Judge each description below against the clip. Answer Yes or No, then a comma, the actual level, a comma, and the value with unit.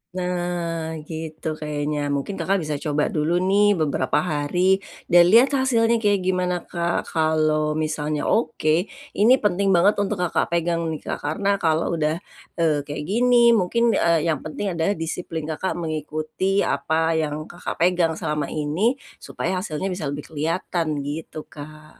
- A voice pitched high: No, medium, 165 Hz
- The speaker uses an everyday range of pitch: Yes, average, 3.4 semitones